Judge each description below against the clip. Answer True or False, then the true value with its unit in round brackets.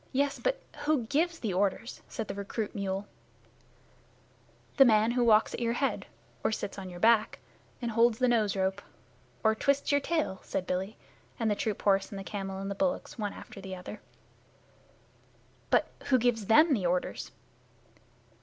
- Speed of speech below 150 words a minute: False (175 wpm)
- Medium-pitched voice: False (220 Hz)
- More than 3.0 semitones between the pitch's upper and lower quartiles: True (4.1 semitones)